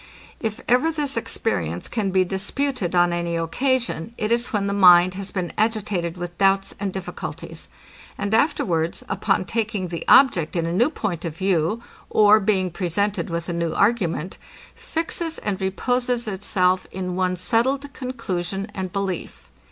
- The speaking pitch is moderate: No, high, 195 Hz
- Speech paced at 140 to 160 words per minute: Yes, average, 155 wpm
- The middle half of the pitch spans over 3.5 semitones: Yes, average, 4.4 semitones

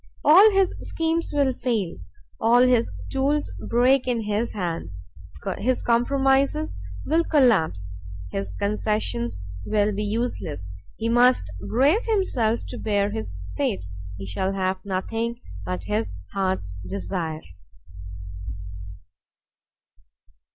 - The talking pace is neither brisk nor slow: No, slow, 110 wpm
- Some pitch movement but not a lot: No, wide, 8.5 semitones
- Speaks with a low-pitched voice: No, high, 215 Hz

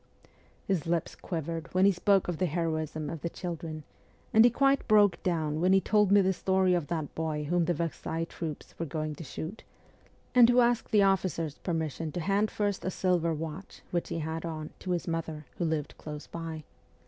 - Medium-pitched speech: Yes, medium, 170 Hz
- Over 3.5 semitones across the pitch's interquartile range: No, average, 3.2 semitones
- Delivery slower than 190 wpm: No, fast, 205 wpm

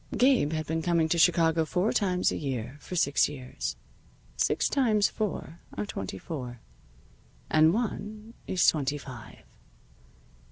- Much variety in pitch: Yes, wide, 5.9 semitones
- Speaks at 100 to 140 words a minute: Yes, slow, 135 wpm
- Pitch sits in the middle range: Yes, medium, 160 Hz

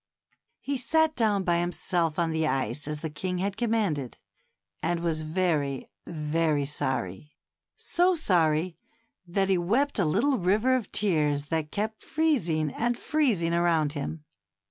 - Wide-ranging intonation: Yes, wide, 5.9 semitones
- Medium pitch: Yes, medium, 170 Hz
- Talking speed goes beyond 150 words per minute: No, average, 145 wpm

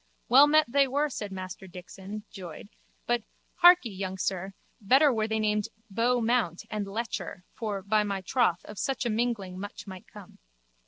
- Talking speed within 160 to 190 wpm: Yes, average, 170 wpm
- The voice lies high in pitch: Yes, high, 210 Hz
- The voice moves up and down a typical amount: Yes, average, 4.0 semitones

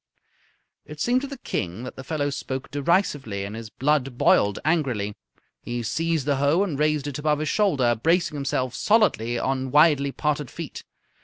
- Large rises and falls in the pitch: No, average, 3.8 semitones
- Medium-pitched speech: Yes, medium, 145 Hz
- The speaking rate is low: No, average, 170 wpm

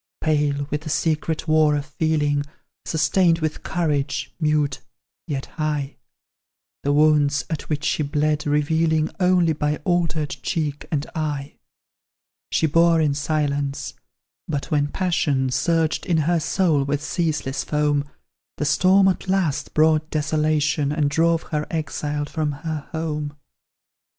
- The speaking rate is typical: No, slow, 130 wpm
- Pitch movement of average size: No, narrow, 1.6 semitones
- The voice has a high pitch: No, medium, 150 Hz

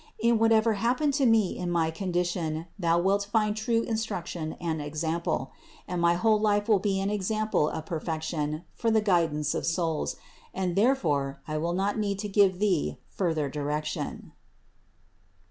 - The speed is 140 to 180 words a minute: Yes, average, 160 wpm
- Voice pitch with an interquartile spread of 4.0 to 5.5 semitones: Yes, average, 4.9 semitones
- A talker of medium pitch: Yes, medium, 180 Hz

